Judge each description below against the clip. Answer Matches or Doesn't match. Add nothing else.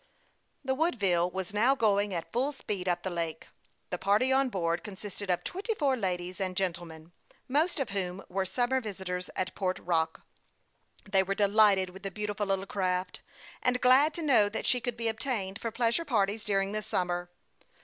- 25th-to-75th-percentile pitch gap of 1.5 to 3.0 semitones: Doesn't match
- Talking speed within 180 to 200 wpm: Matches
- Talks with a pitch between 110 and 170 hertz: Doesn't match